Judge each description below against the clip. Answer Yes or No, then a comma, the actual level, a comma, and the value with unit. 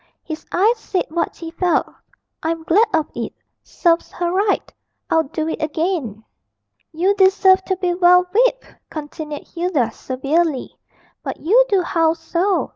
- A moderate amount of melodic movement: Yes, average, 3.0 semitones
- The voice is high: Yes, very high, 340 Hz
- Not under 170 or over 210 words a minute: No, average, 145 wpm